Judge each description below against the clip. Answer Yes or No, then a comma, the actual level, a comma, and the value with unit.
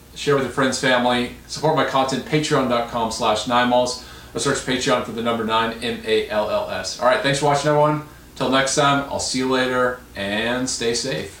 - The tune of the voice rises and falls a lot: No, average, 2.7 semitones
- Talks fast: No, average, 180 wpm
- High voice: No, low, 130 Hz